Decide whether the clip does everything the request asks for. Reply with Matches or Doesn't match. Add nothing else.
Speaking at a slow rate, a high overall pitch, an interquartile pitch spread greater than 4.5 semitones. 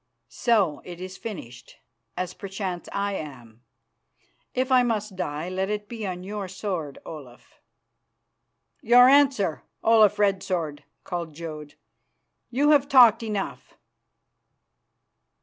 Matches